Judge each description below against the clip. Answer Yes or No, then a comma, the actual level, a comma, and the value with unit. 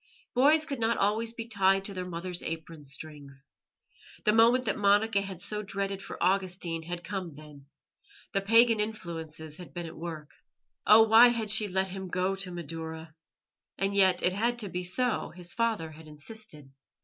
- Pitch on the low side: No, high, 190 Hz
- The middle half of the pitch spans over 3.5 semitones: Yes, average, 4.7 semitones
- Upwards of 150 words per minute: Yes, average, 175 wpm